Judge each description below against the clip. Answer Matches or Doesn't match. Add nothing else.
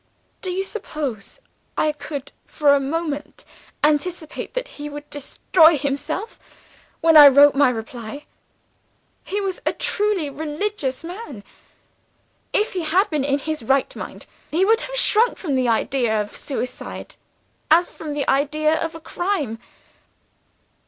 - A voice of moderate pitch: Doesn't match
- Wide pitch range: Doesn't match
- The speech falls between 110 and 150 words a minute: Matches